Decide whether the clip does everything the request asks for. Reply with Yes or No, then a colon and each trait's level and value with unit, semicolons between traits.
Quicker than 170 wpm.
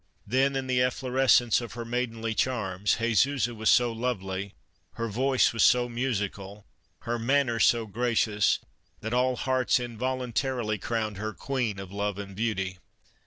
No: average, 145 wpm